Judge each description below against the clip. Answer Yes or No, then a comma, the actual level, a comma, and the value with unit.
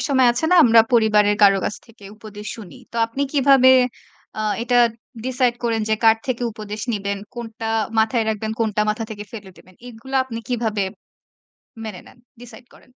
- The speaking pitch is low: No, high, 225 Hz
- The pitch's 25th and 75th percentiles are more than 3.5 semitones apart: No, narrow, 2.5 semitones